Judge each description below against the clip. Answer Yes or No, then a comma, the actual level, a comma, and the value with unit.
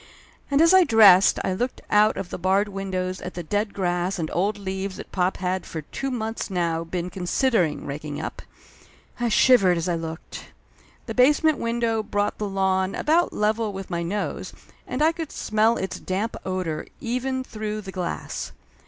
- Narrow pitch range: No, average, 4.0 semitones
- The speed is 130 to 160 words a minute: No, average, 185 wpm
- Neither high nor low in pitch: No, high, 195 Hz